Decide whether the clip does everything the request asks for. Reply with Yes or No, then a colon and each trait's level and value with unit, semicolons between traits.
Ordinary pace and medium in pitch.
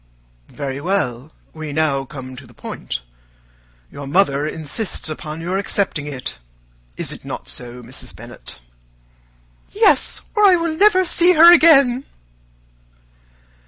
No: slow, 125 wpm; medium, 160 Hz